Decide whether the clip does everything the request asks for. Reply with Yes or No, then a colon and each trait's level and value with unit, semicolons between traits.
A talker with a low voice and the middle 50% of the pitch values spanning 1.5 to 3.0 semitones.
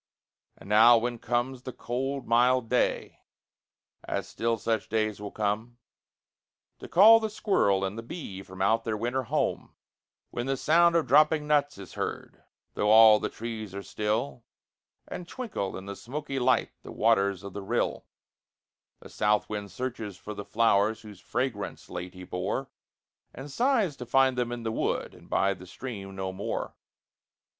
No: low, 115 Hz; average, 4.4 semitones